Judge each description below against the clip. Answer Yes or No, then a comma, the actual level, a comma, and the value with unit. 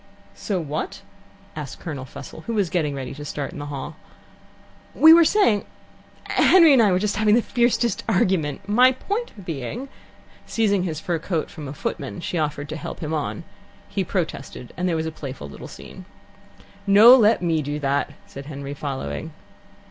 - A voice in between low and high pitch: Yes, medium, 165 Hz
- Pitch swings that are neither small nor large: No, wide, 6.5 semitones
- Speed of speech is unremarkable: Yes, average, 180 wpm